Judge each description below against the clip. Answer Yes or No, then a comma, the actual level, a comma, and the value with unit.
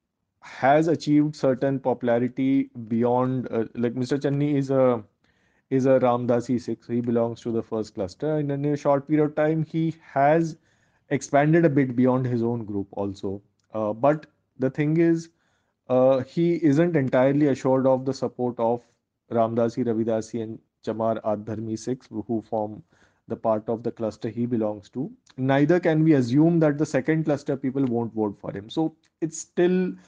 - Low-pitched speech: Yes, low, 130 Hz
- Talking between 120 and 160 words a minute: No, average, 170 wpm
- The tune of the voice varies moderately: Yes, average, 4.3 semitones